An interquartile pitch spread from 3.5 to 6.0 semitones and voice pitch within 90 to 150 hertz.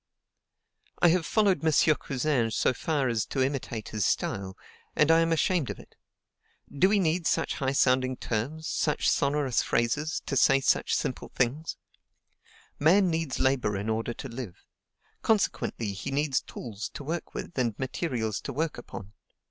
Yes: average, 5.2 semitones; low, 135 Hz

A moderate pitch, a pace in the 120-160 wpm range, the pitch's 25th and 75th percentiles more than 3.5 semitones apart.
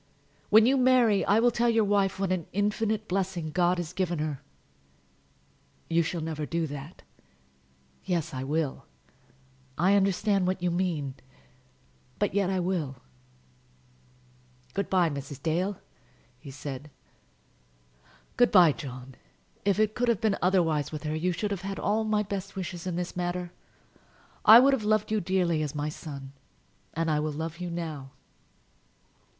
Yes: medium, 180 Hz; average, 155 wpm; average, 4.4 semitones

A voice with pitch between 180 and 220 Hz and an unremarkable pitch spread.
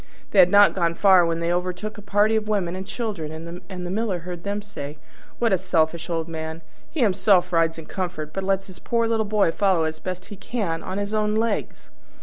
Yes: medium, 185 Hz; average, 3.7 semitones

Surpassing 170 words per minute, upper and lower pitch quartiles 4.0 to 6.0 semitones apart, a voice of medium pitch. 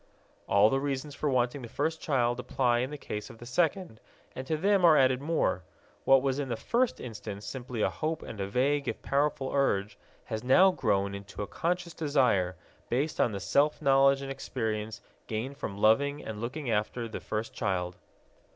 No: average, 190 wpm; average, 4.7 semitones; low, 130 Hz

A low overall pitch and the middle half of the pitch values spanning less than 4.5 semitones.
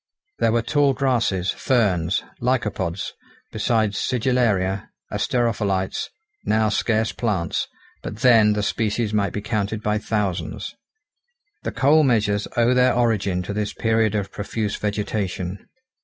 Yes: low, 105 Hz; average, 2.8 semitones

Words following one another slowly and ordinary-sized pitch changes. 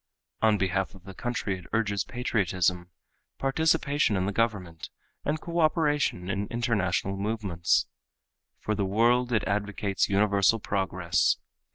Yes: slow, 125 wpm; average, 3.7 semitones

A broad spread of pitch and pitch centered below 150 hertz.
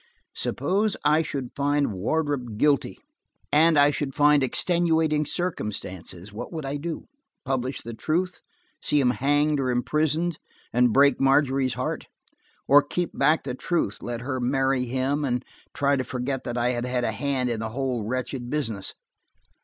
No: average, 3.2 semitones; low, 135 Hz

